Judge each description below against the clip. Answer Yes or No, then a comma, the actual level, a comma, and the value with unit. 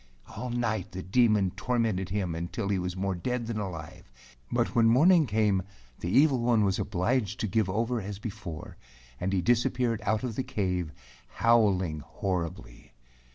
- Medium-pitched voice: No, low, 105 Hz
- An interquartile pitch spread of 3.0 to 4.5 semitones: Yes, average, 4.0 semitones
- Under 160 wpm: No, average, 165 wpm